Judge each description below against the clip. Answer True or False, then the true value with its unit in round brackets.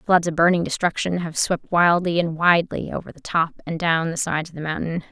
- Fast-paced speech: True (225 wpm)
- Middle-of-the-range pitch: True (165 Hz)